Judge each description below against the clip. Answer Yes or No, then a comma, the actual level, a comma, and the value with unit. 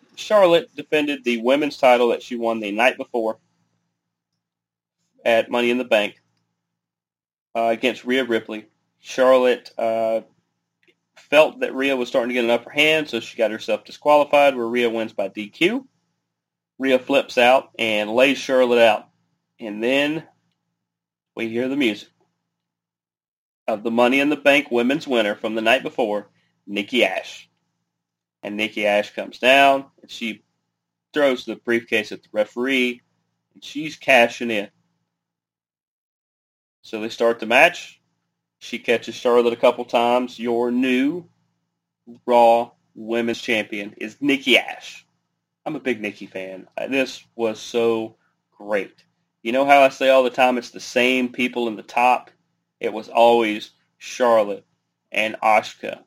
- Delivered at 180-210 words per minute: No, average, 145 wpm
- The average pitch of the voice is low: Yes, low, 120 Hz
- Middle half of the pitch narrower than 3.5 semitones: Yes, average, 2.8 semitones